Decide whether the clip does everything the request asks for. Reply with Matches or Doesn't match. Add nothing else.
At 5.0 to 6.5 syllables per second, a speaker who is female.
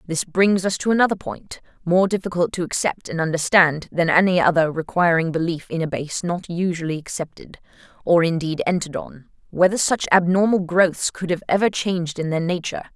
Matches